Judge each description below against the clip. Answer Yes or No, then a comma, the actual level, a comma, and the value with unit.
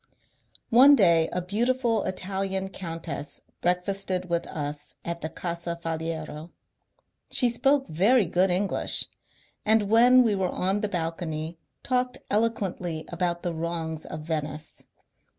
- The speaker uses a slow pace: Yes, slow, 125 wpm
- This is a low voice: No, medium, 180 Hz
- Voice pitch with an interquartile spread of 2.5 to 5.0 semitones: Yes, average, 4.2 semitones